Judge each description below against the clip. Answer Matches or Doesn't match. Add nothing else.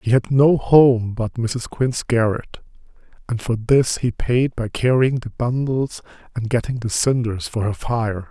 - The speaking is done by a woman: Doesn't match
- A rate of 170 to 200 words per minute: Matches